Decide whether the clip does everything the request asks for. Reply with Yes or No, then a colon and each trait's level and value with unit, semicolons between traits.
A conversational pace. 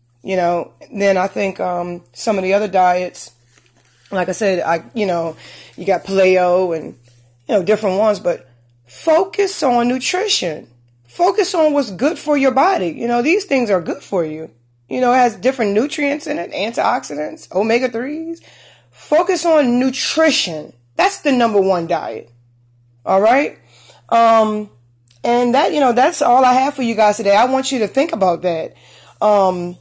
Yes: average, 170 wpm